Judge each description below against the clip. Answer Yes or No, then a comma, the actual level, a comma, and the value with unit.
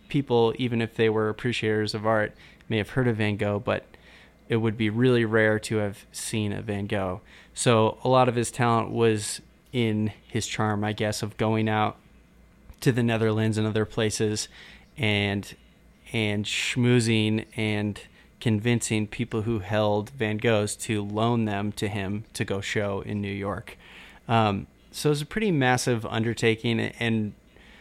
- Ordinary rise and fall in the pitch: No, narrow, 1.8 semitones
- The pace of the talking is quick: No, average, 170 wpm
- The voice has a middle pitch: No, low, 110 Hz